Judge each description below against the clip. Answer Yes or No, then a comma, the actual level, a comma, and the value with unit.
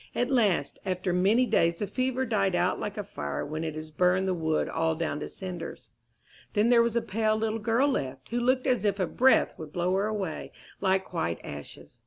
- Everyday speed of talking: No, fast, 215 wpm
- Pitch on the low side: No, high, 190 Hz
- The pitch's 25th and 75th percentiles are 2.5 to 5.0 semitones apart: No, wide, 5.4 semitones